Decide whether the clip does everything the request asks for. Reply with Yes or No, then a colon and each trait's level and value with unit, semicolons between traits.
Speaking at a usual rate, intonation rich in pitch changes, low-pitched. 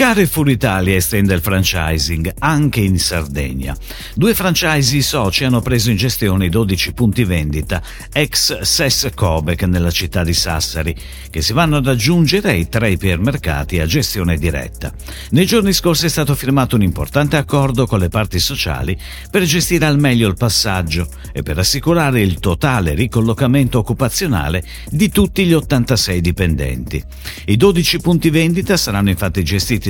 Yes: average, 150 wpm; wide, 8.5 semitones; low, 105 Hz